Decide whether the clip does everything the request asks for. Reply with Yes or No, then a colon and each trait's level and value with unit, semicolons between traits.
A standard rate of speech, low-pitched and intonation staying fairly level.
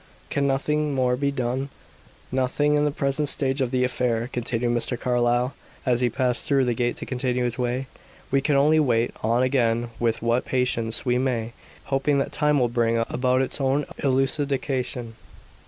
Yes: average, 175 wpm; low, 125 Hz; narrow, 2.3 semitones